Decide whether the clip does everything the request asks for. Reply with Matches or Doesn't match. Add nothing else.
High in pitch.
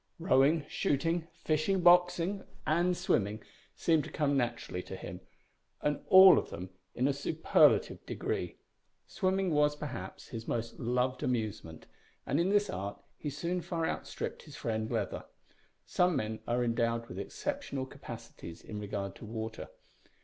Doesn't match